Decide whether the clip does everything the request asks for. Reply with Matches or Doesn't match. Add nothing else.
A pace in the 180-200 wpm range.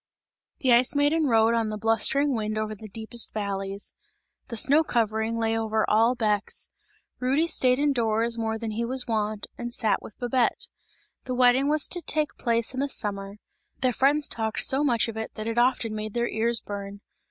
Matches